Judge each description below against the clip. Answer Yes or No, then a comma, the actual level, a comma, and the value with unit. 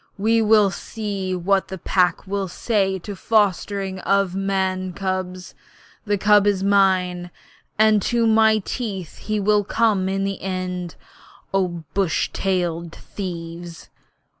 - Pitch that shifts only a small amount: Yes, narrow, 2.0 semitones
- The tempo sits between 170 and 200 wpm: No, slow, 135 wpm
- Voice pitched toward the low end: No, high, 195 Hz